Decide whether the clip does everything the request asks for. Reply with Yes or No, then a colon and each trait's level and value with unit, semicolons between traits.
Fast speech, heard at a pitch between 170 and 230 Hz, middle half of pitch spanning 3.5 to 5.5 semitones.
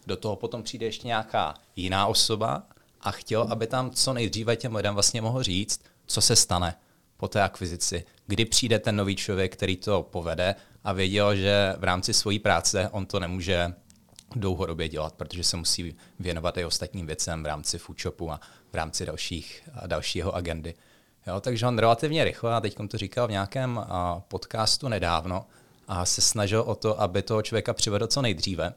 No: fast, 175 wpm; low, 100 Hz; average, 4.0 semitones